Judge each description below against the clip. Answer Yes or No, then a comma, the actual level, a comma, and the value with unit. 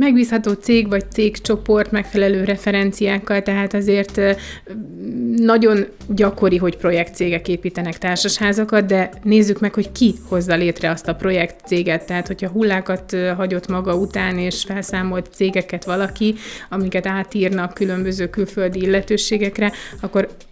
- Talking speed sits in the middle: Yes, average, 115 wpm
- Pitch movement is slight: Yes, narrow, 2.3 semitones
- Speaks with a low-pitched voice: No, high, 195 Hz